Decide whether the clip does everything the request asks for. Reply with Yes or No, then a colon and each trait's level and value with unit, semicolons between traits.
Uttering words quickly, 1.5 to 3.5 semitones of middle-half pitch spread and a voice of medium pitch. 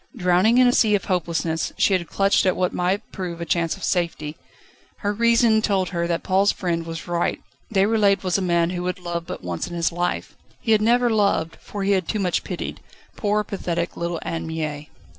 Yes: fast, 210 wpm; average, 3.2 semitones; medium, 180 Hz